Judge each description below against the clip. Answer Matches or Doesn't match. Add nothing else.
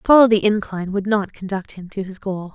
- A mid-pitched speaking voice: Doesn't match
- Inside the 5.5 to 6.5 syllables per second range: Matches